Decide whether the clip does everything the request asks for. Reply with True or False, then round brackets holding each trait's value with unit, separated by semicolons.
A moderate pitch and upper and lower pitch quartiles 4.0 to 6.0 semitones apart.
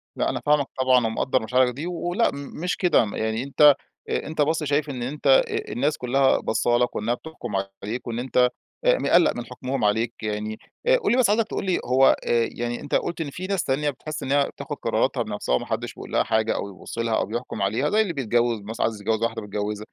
False (130 Hz; 5.2 semitones)